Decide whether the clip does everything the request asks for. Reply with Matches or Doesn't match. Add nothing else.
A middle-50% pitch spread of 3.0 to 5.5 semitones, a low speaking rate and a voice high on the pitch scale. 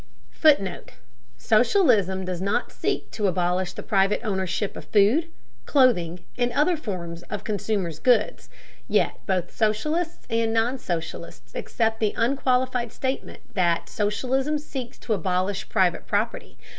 Matches